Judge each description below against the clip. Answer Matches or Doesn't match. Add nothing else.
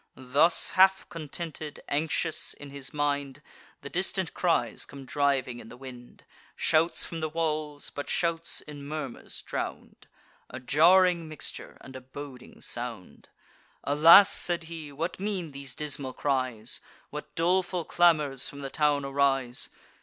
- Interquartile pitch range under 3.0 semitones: Doesn't match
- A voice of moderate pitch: Matches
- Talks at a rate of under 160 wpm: Matches